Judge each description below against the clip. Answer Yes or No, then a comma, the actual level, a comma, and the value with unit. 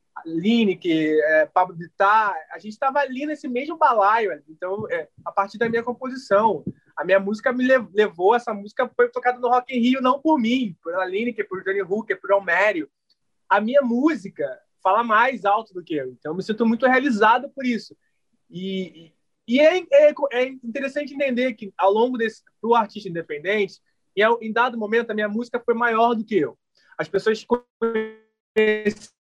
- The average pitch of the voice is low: No, high, 225 Hz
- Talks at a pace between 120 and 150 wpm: No, fast, 185 wpm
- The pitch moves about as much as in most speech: Yes, average, 4.3 semitones